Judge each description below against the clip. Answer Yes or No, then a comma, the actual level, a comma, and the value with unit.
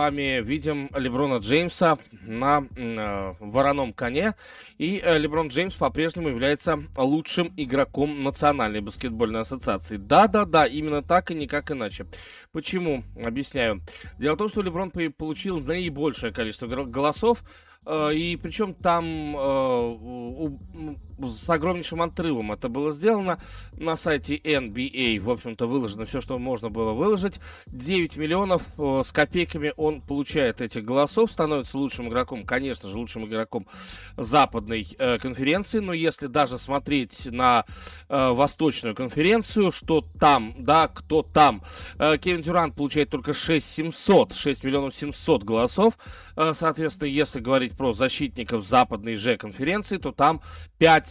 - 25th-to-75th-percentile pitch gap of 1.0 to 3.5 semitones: No, average, 4.5 semitones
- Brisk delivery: No, average, 135 wpm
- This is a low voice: No, medium, 145 Hz